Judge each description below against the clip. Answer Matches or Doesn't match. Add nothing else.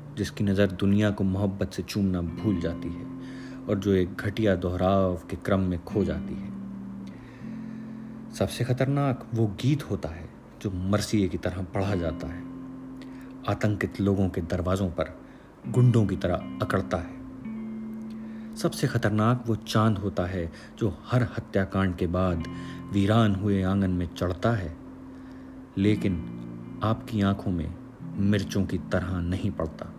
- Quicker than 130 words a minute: Matches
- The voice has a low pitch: Matches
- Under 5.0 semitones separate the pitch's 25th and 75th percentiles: Doesn't match